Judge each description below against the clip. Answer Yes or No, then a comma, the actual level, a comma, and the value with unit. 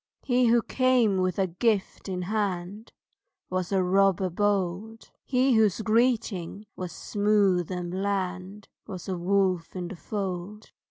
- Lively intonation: No, average, 2.9 semitones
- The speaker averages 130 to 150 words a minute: Yes, average, 140 wpm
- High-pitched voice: Yes, high, 195 Hz